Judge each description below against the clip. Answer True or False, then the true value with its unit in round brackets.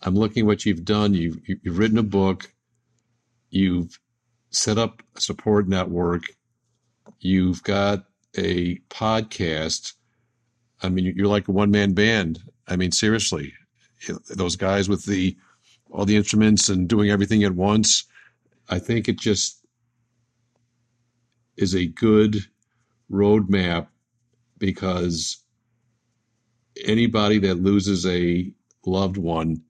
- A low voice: True (105 Hz)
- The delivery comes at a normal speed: False (120 wpm)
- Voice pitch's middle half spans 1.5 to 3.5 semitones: False (3.9 semitones)